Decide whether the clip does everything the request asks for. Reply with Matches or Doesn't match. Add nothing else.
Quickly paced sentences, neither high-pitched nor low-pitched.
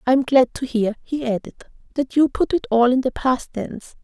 Doesn't match